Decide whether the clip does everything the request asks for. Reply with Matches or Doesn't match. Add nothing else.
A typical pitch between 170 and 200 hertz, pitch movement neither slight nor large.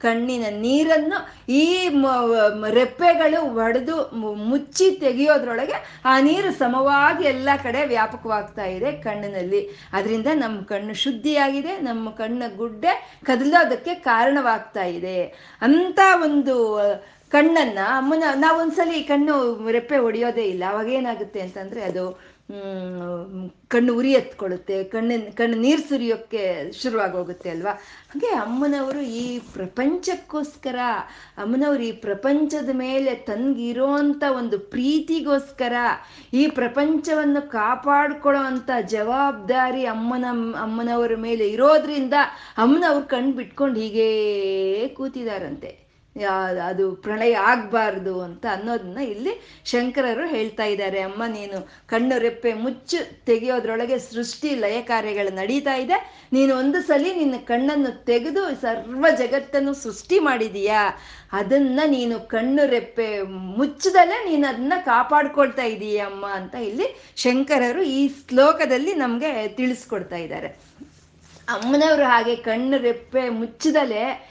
Doesn't match